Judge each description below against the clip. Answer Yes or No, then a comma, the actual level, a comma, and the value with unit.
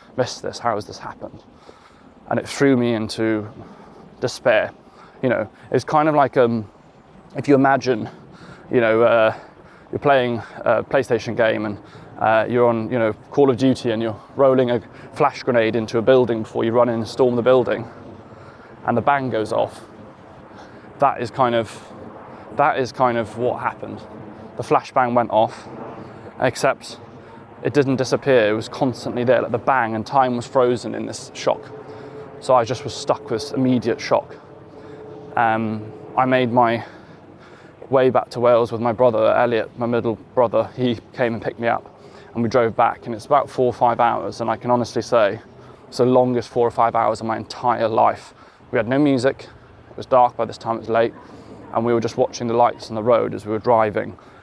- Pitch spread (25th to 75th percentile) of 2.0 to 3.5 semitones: Yes, narrow, 2.5 semitones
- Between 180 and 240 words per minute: Yes, average, 195 wpm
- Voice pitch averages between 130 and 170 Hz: No, low, 120 Hz